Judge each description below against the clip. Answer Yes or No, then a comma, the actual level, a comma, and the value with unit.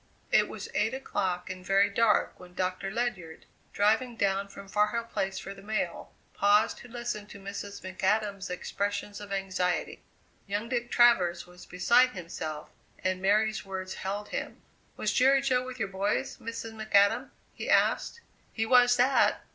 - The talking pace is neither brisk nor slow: Yes, average, 160 wpm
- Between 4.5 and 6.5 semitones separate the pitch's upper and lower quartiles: No, average, 3.2 semitones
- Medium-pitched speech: No, high, 205 Hz